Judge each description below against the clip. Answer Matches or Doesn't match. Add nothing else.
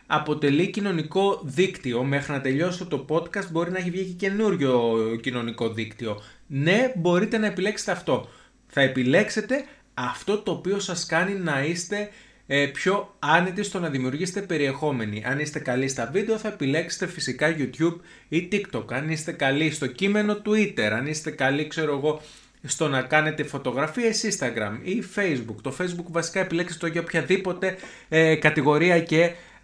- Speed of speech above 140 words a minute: Matches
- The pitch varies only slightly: Doesn't match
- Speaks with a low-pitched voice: Doesn't match